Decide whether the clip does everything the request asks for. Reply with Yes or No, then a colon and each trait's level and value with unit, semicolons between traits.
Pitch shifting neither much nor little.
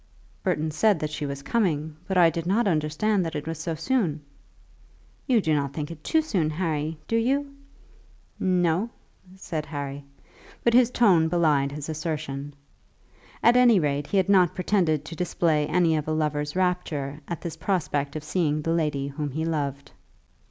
Yes: average, 3.7 semitones